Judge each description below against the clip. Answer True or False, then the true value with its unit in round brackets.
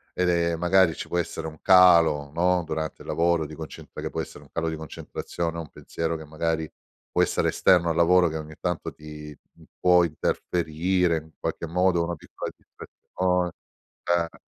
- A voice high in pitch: False (85 Hz)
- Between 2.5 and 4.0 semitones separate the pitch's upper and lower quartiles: False (2.0 semitones)